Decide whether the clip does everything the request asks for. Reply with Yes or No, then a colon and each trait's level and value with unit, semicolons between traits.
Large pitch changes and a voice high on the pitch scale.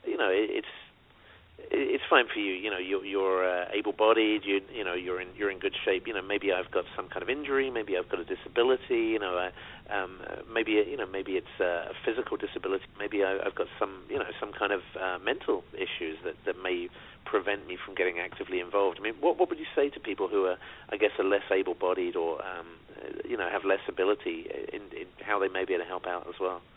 No: average, 4.7 semitones; very high, 390 Hz